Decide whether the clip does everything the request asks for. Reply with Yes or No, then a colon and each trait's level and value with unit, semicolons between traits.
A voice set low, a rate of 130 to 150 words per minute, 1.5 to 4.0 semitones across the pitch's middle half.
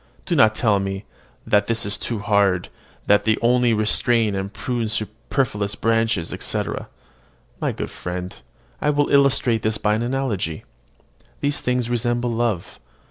Yes: low, 110 Hz; average, 145 wpm; average, 2.9 semitones